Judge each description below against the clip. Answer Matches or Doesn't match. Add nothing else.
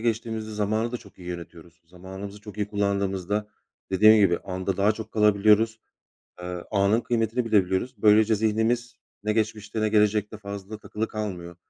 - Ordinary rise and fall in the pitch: Doesn't match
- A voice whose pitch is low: Matches